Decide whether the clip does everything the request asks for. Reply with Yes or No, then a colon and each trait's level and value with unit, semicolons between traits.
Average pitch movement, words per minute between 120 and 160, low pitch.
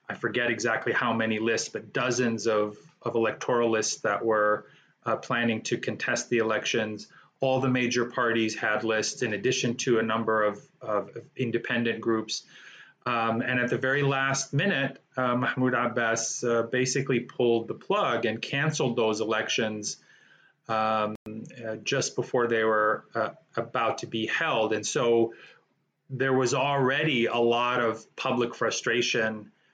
No: narrow, 2.3 semitones; average, 150 wpm; low, 115 Hz